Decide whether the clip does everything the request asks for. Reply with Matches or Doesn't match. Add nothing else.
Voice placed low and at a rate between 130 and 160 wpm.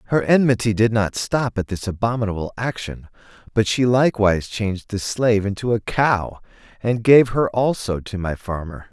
Doesn't match